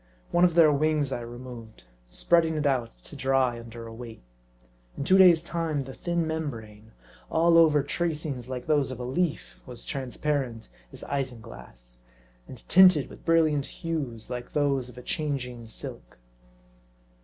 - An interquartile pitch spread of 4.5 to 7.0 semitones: Yes, average, 5.0 semitones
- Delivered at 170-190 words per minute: No, average, 155 wpm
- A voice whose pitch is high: No, low, 135 Hz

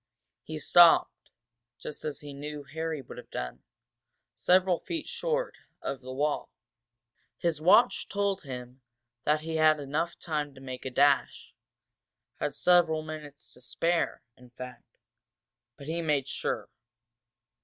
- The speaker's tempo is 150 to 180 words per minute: No, slow, 135 wpm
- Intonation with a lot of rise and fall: No, average, 3.7 semitones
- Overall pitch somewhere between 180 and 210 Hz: No, medium, 150 Hz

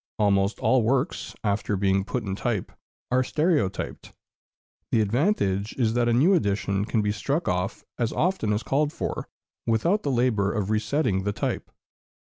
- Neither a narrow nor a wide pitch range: Yes, average, 4.6 semitones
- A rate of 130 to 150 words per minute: No, average, 160 wpm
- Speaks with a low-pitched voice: Yes, low, 110 Hz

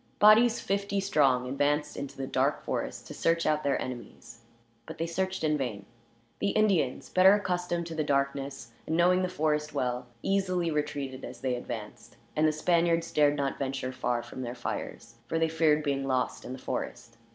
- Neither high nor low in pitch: Yes, medium, 150 Hz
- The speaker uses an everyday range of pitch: Yes, average, 4.6 semitones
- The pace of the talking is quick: No, average, 185 wpm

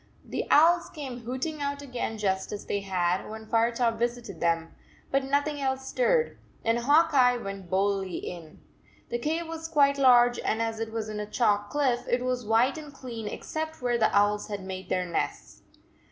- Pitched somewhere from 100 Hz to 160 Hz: No, high, 240 Hz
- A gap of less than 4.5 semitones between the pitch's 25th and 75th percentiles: No, average, 5.3 semitones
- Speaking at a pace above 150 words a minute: Yes, average, 185 wpm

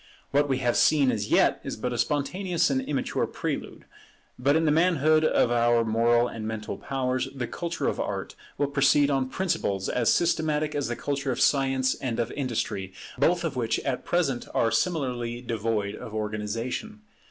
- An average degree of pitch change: Yes, average, 4.1 semitones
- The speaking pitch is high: No, low, 130 Hz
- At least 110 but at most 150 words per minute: No, average, 175 wpm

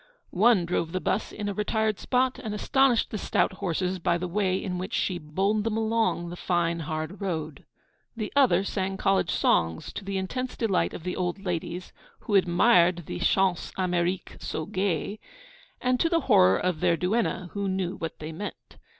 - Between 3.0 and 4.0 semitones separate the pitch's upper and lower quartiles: Yes, average, 3.4 semitones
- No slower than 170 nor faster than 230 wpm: Yes, average, 185 wpm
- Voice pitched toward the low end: No, medium, 185 Hz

